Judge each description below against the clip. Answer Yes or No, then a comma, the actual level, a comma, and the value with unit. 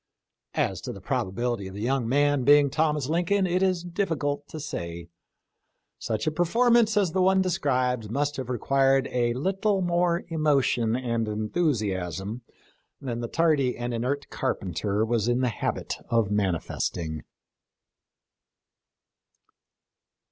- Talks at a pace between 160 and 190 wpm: No, slow, 135 wpm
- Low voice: Yes, low, 130 Hz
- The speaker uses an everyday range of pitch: No, wide, 6.4 semitones